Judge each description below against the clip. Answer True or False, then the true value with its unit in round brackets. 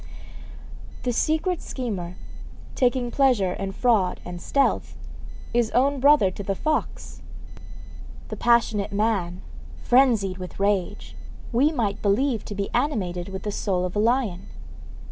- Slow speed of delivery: True (130 wpm)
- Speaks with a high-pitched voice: True (215 Hz)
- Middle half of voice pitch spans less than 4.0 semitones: False (4.7 semitones)